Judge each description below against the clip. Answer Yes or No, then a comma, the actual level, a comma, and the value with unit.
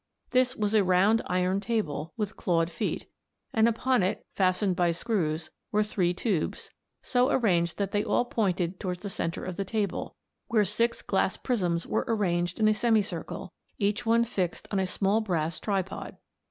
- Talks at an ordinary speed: Yes, average, 170 wpm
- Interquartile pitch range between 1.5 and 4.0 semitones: Yes, average, 3.6 semitones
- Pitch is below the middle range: No, high, 200 Hz